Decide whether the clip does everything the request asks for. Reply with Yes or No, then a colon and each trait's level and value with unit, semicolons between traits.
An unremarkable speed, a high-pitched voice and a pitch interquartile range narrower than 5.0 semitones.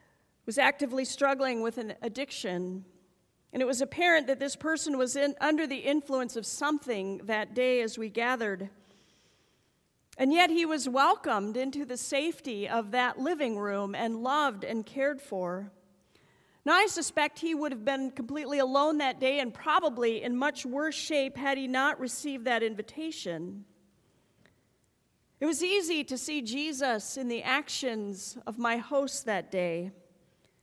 Yes: average, 155 wpm; very high, 260 Hz; average, 4.3 semitones